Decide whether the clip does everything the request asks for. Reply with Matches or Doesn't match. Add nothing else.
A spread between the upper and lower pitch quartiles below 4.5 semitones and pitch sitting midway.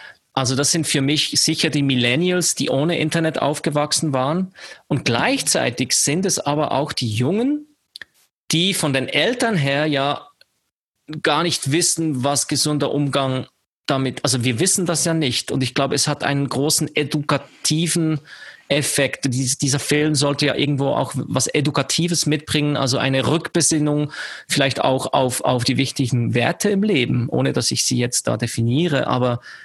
Matches